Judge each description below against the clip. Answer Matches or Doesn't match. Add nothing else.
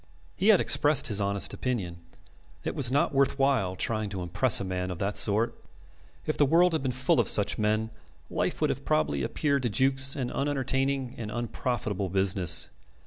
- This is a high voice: Doesn't match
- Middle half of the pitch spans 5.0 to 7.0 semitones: Matches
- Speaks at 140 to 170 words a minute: Doesn't match